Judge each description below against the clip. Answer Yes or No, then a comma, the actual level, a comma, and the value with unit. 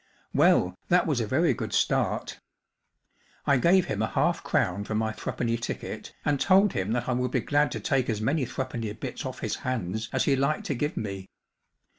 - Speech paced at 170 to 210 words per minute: Yes, average, 200 wpm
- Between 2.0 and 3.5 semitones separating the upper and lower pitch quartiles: No, average, 4.8 semitones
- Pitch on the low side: Yes, low, 125 Hz